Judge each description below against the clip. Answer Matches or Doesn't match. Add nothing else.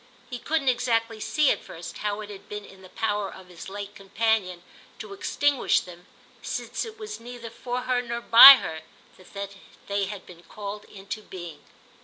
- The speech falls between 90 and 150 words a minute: Doesn't match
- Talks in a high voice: Matches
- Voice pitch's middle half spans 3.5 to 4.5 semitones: Matches